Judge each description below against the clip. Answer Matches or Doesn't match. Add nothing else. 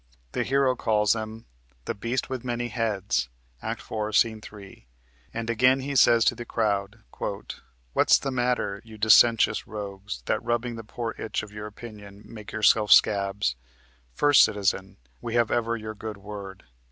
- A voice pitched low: Matches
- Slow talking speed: Doesn't match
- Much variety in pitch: Doesn't match